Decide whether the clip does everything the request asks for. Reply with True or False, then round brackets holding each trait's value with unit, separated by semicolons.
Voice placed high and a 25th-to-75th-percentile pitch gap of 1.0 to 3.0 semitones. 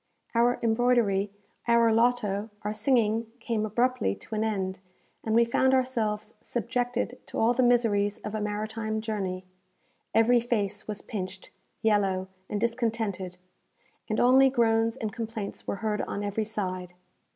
True (220 Hz; 2.4 semitones)